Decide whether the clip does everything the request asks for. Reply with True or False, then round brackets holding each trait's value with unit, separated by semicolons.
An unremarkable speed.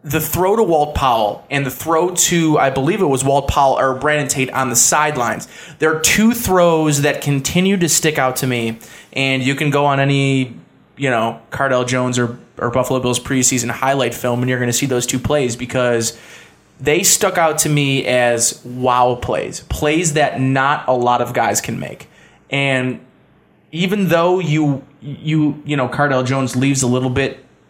True (190 wpm)